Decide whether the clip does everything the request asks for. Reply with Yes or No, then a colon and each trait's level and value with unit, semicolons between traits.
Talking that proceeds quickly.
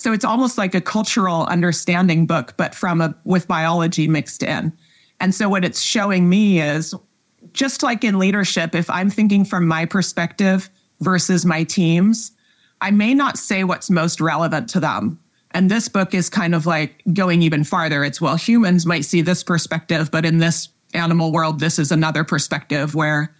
No: average, 180 wpm